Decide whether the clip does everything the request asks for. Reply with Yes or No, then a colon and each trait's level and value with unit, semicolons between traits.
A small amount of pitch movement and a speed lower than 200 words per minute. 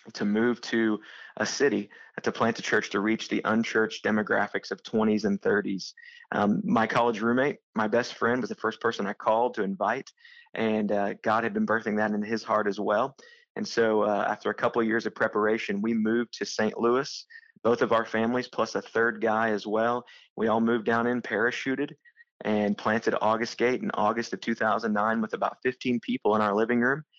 No: narrow, 2.2 semitones; fast, 205 wpm